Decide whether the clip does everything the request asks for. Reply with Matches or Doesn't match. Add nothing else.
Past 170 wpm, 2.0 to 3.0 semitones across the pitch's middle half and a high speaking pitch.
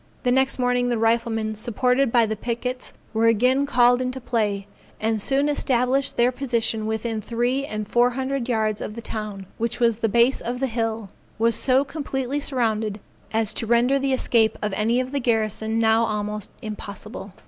Matches